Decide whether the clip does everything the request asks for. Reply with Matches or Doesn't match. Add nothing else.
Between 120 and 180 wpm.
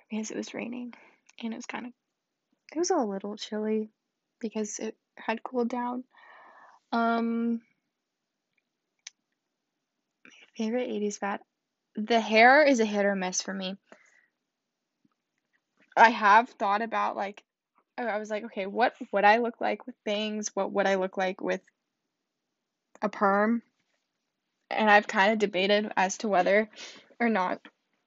Matches